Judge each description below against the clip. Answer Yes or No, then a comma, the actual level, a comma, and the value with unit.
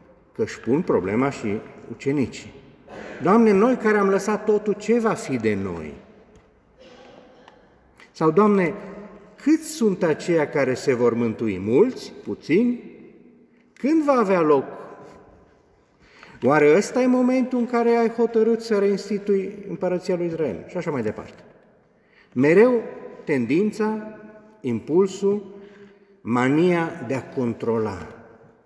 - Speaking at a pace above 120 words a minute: No, slow, 115 wpm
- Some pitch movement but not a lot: No, wide, 7.8 semitones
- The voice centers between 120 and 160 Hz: No, high, 200 Hz